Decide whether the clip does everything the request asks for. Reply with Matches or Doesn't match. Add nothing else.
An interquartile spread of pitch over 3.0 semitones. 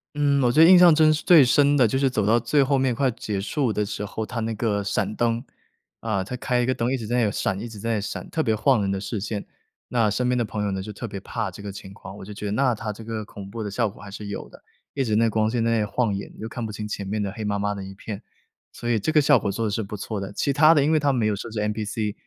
Matches